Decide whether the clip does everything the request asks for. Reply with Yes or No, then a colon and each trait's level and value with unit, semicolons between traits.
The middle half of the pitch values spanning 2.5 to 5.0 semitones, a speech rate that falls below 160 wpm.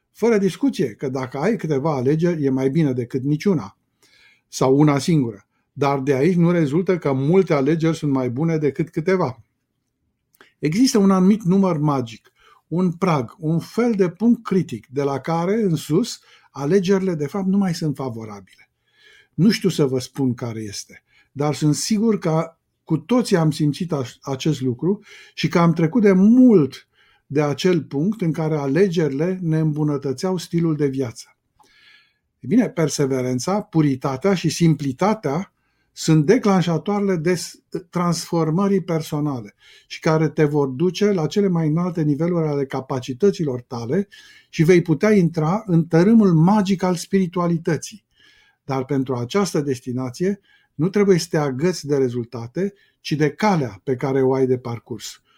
No: wide, 5.4 semitones; average, 150 wpm